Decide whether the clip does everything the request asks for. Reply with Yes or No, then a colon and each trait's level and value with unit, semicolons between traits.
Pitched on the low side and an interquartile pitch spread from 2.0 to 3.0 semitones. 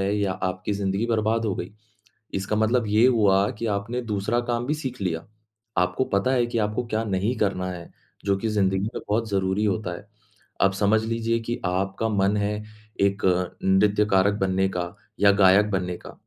Yes: low, 100 Hz; average, 2.7 semitones